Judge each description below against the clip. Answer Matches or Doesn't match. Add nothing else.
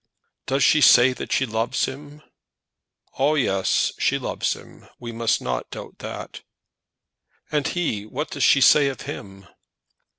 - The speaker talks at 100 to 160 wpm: Matches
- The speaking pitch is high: Doesn't match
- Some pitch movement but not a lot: Matches